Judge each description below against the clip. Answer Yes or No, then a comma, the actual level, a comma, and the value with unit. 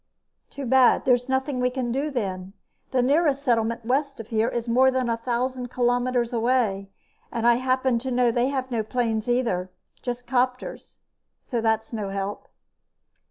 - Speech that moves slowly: No, average, 165 wpm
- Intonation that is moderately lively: No, narrow, 2.1 semitones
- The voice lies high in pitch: Yes, high, 245 Hz